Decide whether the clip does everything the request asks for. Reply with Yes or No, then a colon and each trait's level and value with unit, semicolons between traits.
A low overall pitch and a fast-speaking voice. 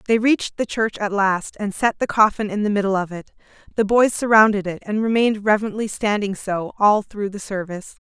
No: high, 205 Hz; fast, 210 wpm